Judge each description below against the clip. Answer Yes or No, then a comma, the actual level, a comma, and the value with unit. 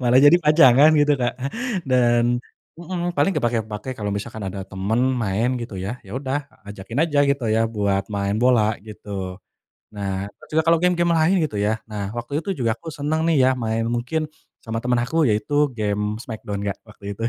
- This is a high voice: No, low, 120 Hz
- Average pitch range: No, wide, 5.7 semitones